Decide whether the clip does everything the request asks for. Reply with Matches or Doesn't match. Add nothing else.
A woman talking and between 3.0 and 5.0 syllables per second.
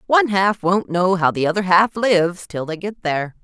Doesn't match